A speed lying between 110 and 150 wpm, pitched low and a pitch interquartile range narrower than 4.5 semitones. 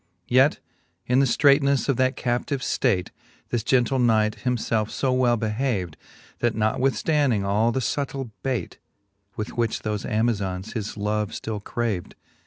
Yes: average, 145 wpm; low, 120 Hz; average, 3.4 semitones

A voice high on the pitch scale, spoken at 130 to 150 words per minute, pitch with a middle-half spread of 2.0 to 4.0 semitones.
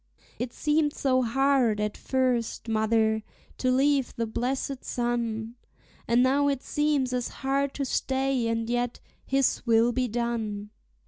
Yes: high, 245 Hz; average, 140 wpm; average, 2.8 semitones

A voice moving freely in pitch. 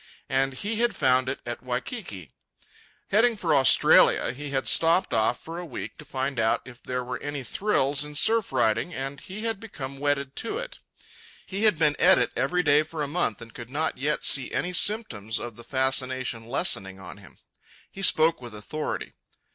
Yes: wide, 5.7 semitones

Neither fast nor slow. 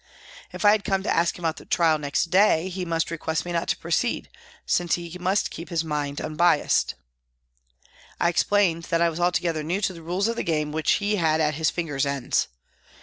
No: fast, 215 wpm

